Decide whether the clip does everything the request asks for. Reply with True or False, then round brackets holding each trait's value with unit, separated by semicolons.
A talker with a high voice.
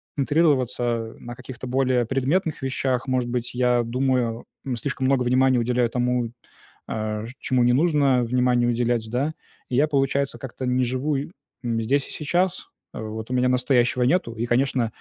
False (125 Hz)